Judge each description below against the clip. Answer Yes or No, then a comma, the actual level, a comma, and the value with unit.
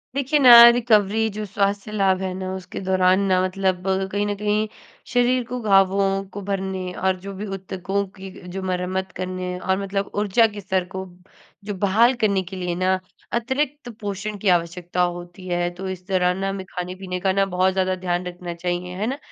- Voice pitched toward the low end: No, high, 190 Hz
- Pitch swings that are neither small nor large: No, narrow, 1.9 semitones